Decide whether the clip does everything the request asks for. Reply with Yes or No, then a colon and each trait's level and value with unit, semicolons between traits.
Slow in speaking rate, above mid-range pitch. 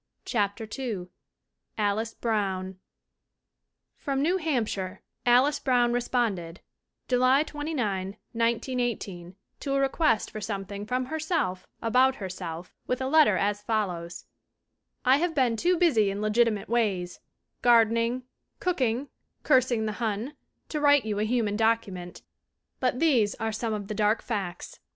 Yes: slow, 130 wpm; high, 230 Hz